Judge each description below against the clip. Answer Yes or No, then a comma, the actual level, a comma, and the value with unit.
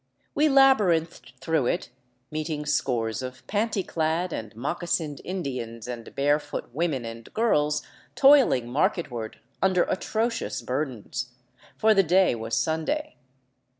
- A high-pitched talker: No, medium, 155 Hz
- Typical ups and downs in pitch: No, wide, 6.9 semitones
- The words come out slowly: Yes, slow, 120 wpm